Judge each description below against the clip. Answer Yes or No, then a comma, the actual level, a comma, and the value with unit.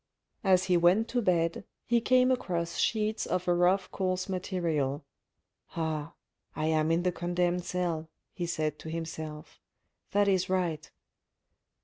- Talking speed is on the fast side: No, average, 145 wpm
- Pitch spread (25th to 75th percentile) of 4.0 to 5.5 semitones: No, narrow, 2.6 semitones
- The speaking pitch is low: No, medium, 175 Hz